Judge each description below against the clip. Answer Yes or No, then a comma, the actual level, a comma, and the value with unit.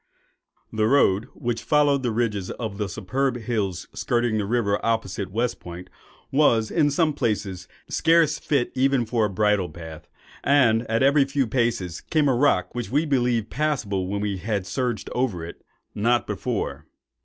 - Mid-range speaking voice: No, low, 115 Hz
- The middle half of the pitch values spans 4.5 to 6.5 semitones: Yes, average, 4.9 semitones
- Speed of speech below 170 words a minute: Yes, average, 160 wpm